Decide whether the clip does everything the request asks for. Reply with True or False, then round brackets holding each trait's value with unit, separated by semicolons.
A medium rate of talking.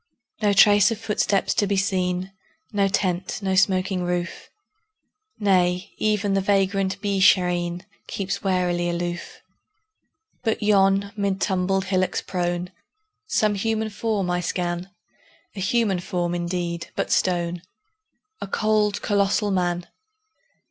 False (120 wpm)